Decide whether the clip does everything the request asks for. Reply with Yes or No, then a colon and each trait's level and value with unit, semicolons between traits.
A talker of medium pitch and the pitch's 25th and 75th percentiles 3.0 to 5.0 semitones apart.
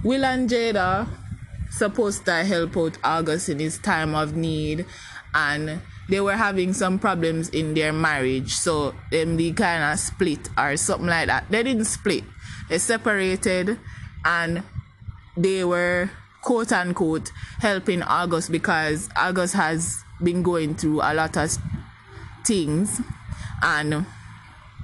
Yes: medium, 165 Hz; average, 4.0 semitones